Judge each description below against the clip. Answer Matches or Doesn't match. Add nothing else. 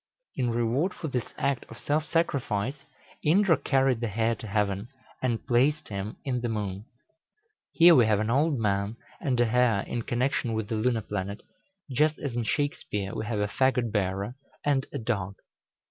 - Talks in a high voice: Doesn't match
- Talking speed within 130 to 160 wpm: Doesn't match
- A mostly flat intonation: Doesn't match